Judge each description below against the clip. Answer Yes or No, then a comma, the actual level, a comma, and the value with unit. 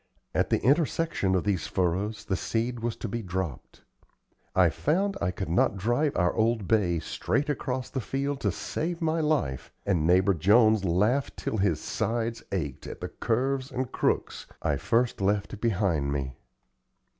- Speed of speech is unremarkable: Yes, average, 165 wpm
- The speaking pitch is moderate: No, low, 110 Hz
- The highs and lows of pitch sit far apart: Yes, wide, 5.8 semitones